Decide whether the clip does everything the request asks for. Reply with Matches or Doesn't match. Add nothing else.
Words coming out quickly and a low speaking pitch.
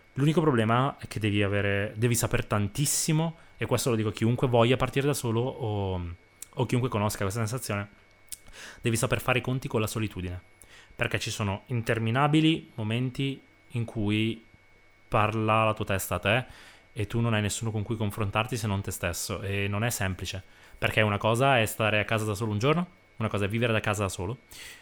Matches